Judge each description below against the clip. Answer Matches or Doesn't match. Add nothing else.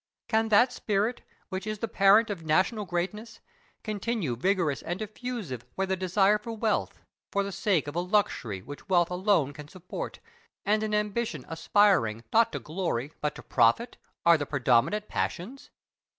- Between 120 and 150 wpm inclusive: Doesn't match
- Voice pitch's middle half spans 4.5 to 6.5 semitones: Matches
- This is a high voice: Matches